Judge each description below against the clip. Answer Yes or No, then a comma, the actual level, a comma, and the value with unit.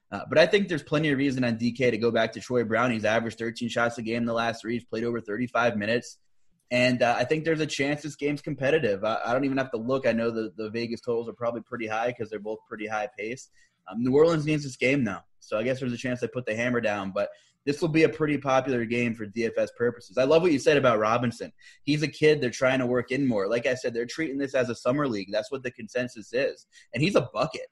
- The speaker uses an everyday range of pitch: Yes, average, 3.3 semitones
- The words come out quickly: Yes, fast, 275 wpm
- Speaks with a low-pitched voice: Yes, low, 120 Hz